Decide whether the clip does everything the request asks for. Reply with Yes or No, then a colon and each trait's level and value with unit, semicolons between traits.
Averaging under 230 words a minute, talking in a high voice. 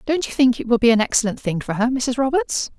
No: fast, 280 wpm; high, 245 Hz